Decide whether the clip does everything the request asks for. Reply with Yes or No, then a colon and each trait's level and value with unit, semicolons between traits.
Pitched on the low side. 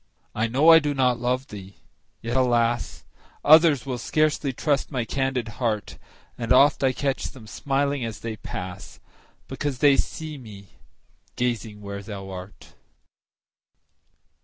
Yes: low, 125 Hz